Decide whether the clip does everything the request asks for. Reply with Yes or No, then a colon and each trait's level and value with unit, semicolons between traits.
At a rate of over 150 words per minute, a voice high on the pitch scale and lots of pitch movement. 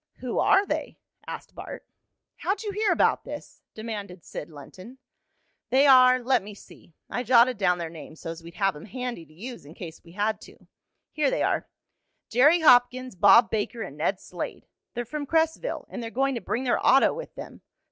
Yes: average, 190 wpm; high, 240 Hz; wide, 5.7 semitones